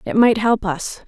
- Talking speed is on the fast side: Yes, fast, 225 wpm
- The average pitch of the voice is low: No, high, 215 Hz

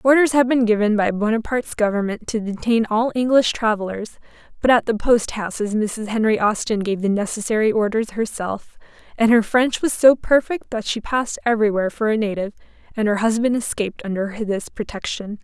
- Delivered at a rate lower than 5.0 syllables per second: No, 5.6 syllables/s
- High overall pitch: Yes, high, 220 Hz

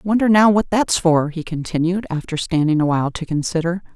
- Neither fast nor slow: Yes, average, 180 wpm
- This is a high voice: No, medium, 175 Hz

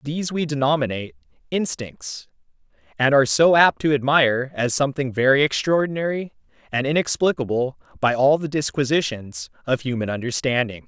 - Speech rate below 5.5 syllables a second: No, 5.6 syllables/s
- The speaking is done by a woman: No, male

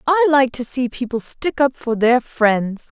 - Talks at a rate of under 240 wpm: Yes, average, 200 wpm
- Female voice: Yes, female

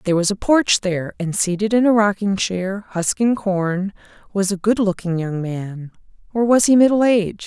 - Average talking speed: Yes, average, 195 wpm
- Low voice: No, high, 200 Hz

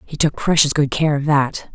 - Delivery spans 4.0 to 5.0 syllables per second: Yes, 4.9 syllables/s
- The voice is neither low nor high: Yes, medium, 145 Hz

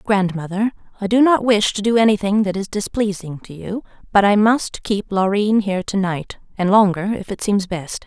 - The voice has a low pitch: No, high, 200 Hz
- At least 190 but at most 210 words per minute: Yes, average, 195 wpm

